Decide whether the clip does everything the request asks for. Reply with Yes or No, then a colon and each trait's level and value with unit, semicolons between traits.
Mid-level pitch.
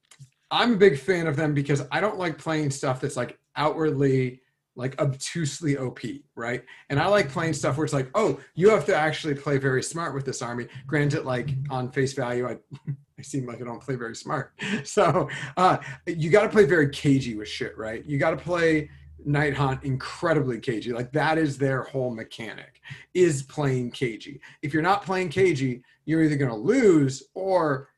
Yes: medium, 145 Hz